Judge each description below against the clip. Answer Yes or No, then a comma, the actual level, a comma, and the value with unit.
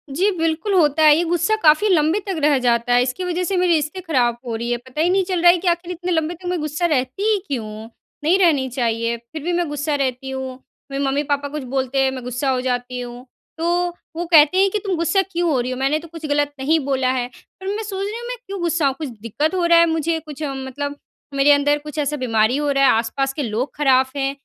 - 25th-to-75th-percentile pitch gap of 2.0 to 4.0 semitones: No, average, 4.7 semitones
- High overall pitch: Yes, very high, 295 Hz